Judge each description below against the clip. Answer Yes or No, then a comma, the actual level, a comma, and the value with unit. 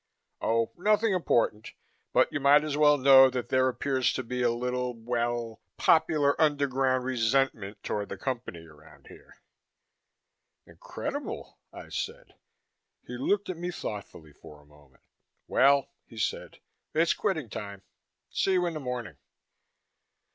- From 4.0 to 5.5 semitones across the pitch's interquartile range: Yes, average, 4.4 semitones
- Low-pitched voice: Yes, low, 125 Hz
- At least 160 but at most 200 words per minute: No, average, 140 wpm